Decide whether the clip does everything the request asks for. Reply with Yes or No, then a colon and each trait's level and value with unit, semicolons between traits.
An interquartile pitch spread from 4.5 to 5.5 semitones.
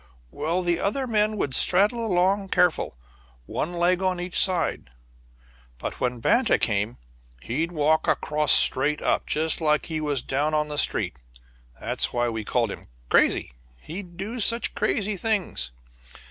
Yes: average, 5.0 semitones